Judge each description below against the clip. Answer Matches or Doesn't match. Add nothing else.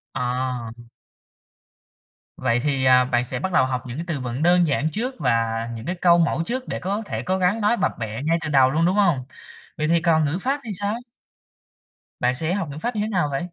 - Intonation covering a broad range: Matches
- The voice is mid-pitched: Matches